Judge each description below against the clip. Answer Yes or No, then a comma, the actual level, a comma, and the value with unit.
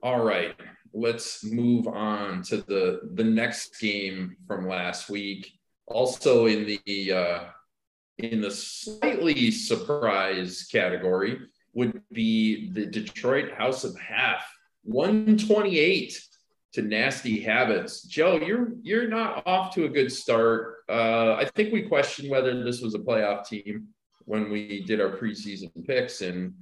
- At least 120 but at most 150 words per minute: Yes, average, 140 wpm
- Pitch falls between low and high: No, low, 115 Hz